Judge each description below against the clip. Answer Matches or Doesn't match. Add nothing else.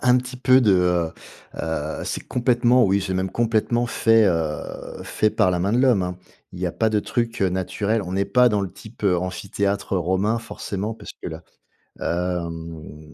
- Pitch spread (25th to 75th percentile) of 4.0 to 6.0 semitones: Matches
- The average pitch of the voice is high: Doesn't match